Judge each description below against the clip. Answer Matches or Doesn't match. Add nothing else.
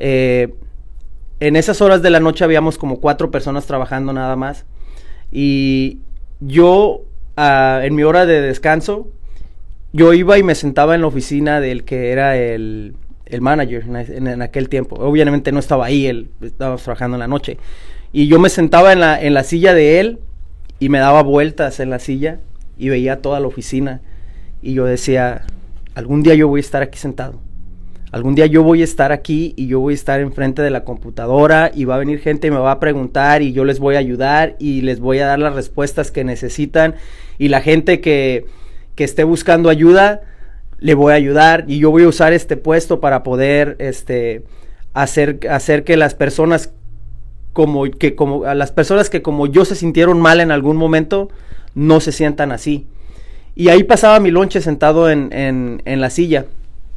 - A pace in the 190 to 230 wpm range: Matches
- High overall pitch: Doesn't match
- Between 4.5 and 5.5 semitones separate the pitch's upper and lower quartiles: Doesn't match